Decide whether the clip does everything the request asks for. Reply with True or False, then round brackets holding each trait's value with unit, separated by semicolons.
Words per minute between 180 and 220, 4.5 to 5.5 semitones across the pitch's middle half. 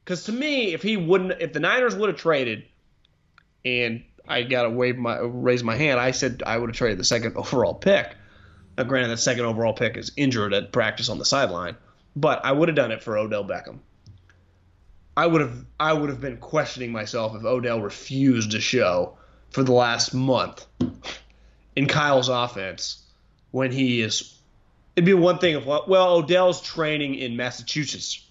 True (185 wpm; 4.9 semitones)